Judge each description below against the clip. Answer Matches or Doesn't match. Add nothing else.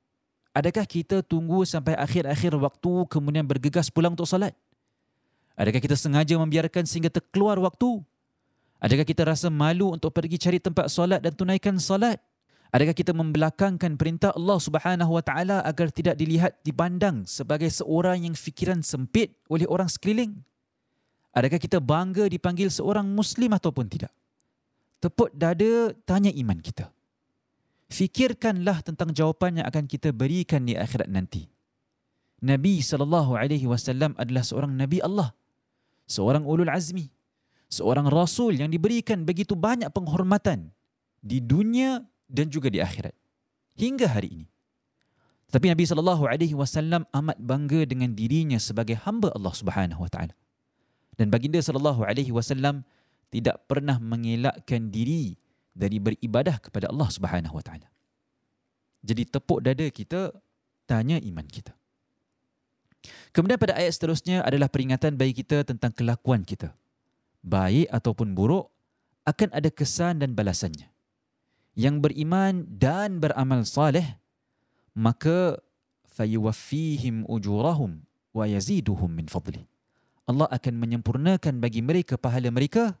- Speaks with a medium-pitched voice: Matches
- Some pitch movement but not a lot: Doesn't match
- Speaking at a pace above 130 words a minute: Doesn't match